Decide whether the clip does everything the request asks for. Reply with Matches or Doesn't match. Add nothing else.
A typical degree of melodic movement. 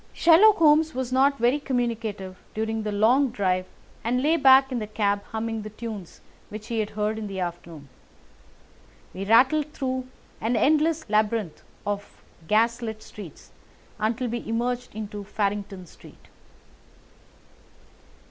Matches